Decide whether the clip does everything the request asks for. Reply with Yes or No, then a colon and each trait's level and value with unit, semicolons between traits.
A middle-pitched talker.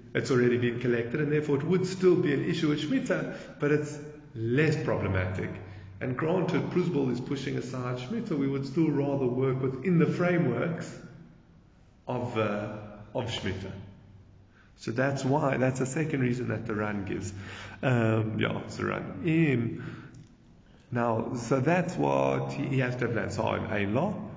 No: low, 125 Hz